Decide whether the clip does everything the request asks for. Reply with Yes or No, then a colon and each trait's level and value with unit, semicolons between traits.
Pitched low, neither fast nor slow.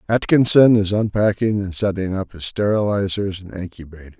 Yes: low, 100 Hz; average, 145 wpm